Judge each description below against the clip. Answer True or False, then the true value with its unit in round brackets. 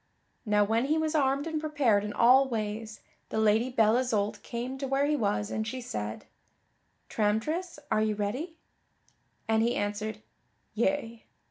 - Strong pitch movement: False (4.4 semitones)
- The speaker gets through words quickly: False (155 wpm)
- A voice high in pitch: True (230 Hz)